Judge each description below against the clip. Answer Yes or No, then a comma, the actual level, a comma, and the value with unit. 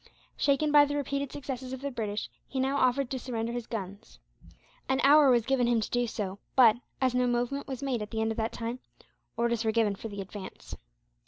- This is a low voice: No, high, 245 Hz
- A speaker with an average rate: No, fast, 220 wpm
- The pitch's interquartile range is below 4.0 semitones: Yes, average, 3.3 semitones